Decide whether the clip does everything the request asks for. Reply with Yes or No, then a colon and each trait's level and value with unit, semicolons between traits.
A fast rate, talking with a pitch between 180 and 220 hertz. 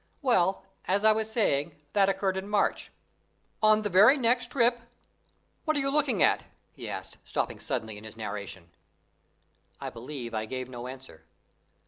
No: average, 160 wpm; high, 190 Hz